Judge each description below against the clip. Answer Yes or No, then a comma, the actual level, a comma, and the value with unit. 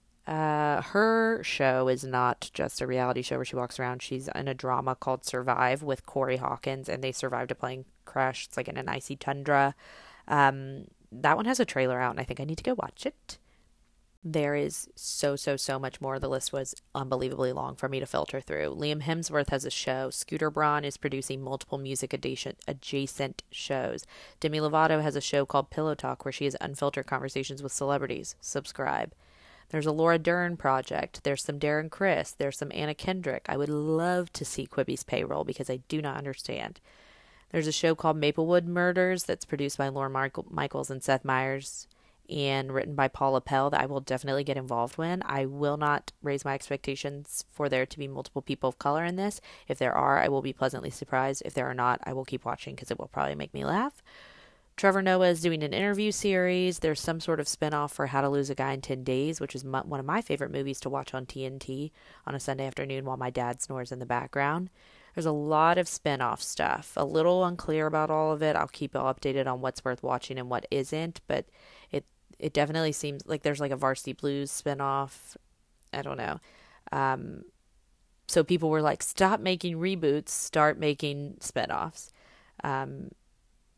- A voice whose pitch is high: No, medium, 140 Hz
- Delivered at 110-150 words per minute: No, fast, 205 wpm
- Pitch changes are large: No, average, 2.7 semitones